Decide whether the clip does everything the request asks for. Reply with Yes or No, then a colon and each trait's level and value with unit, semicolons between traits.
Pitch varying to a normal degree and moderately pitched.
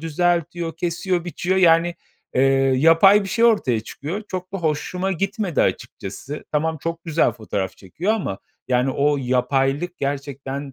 Yes: average, 4.6 semitones; medium, 165 Hz